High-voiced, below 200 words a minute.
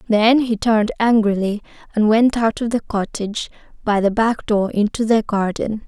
Yes: high, 220 Hz; average, 175 wpm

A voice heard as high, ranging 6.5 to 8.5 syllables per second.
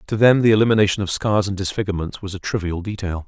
No: low, 100 Hz; 7.0 syllables/s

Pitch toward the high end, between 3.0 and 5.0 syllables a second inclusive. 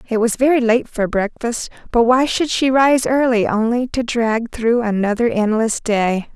Yes: high, 235 Hz; 4.4 syllables/s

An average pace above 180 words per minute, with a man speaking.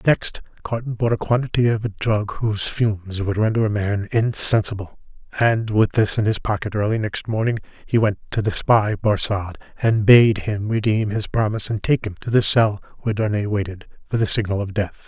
Yes: average, 200 wpm; male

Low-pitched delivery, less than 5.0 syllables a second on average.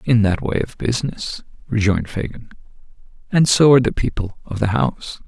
No: low, 115 Hz; 5.6 syllables/s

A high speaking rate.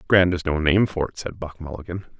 Yes: fast, 245 wpm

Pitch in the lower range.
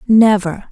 No: high, 205 Hz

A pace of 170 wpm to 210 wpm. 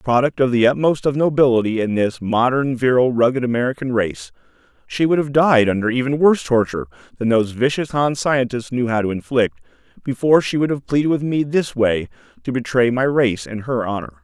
Yes: average, 195 wpm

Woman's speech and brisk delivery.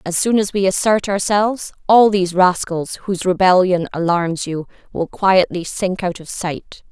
No: female; average, 165 wpm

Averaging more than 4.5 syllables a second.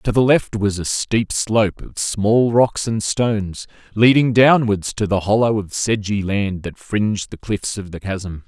No: 4.2 syllables/s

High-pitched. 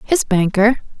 Yes: high, 220 Hz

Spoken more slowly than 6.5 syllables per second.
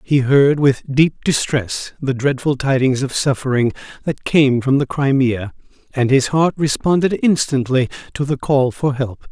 Yes: 4.3 syllables/s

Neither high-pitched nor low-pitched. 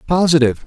Yes: medium, 150 Hz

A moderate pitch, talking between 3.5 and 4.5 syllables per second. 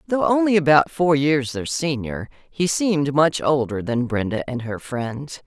Yes: medium, 145 Hz; 4.3 syllables/s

